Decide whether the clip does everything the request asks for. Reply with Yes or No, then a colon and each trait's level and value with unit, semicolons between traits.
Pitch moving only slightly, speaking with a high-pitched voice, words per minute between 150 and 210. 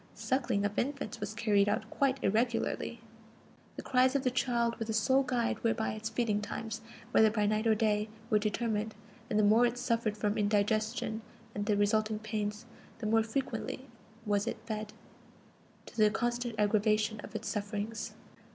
Yes: narrow, 1.9 semitones; high, 220 Hz; average, 170 wpm